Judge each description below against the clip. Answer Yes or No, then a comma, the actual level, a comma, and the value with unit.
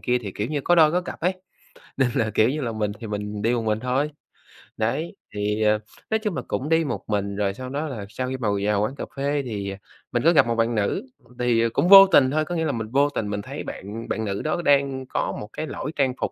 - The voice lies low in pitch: Yes, low, 125 Hz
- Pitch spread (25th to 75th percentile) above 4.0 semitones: Yes, wide, 5.4 semitones